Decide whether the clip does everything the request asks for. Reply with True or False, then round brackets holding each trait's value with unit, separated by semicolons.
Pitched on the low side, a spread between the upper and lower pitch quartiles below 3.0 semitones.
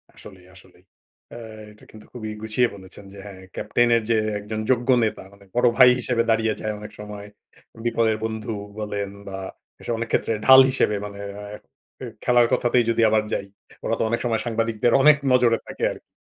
True (110 Hz; 2.4 semitones)